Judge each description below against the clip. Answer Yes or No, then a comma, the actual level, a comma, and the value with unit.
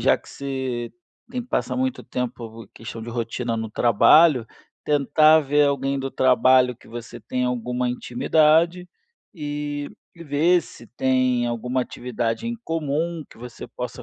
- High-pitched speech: No, low, 130 Hz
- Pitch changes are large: No, average, 3.9 semitones